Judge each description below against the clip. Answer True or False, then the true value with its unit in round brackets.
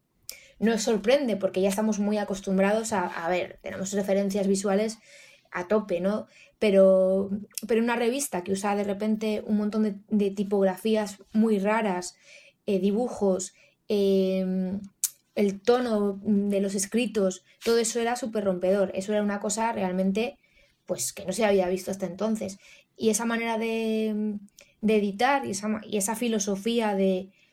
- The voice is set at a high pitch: True (205 Hz)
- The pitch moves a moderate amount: False (2.3 semitones)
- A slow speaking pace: False (150 wpm)